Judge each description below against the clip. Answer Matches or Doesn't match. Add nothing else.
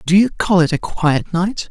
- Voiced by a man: Matches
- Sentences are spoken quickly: Matches